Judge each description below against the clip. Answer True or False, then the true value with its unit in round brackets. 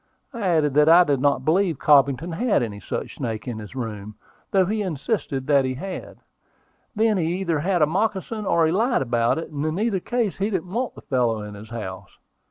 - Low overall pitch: False (160 Hz)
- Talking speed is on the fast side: True (210 wpm)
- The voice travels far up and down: True (7.1 semitones)